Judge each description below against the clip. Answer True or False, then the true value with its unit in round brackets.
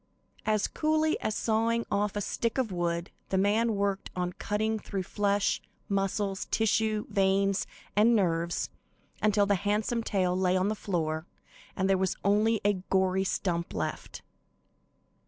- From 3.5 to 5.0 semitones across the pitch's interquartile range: False (2.4 semitones)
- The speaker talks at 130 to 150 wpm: True (145 wpm)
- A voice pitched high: True (200 Hz)